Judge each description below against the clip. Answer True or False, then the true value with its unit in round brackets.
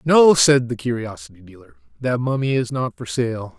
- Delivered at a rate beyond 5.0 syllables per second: False (4.9 syllables/s)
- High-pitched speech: False (125 Hz)